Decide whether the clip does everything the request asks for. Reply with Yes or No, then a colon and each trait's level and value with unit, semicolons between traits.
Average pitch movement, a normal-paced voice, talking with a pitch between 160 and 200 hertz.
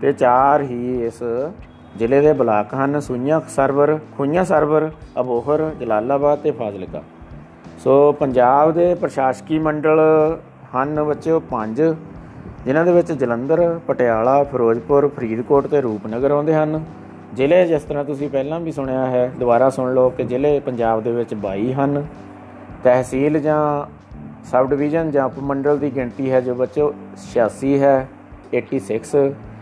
No: average, 3.3 semitones; average, 135 wpm; medium, 140 Hz